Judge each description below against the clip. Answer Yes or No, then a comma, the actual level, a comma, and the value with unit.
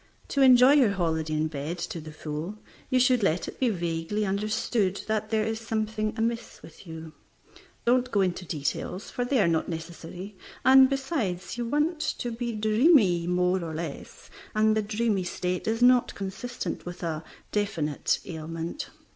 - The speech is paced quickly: No, average, 165 wpm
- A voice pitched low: No, high, 205 Hz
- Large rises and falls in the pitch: Yes, wide, 5.7 semitones